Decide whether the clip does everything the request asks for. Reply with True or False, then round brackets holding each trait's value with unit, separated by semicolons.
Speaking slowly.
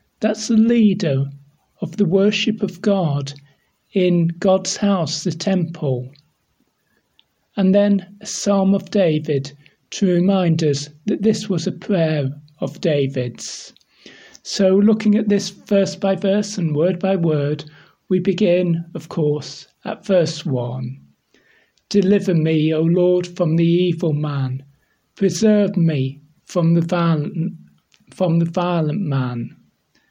True (130 wpm)